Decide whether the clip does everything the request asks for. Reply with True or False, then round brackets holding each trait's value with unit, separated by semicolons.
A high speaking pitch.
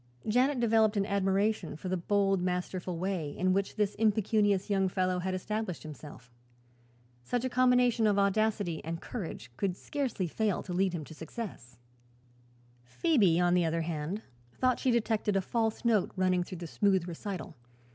True (195 Hz)